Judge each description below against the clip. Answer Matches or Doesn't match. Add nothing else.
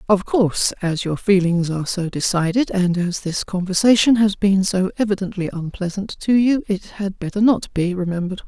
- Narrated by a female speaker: Matches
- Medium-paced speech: Matches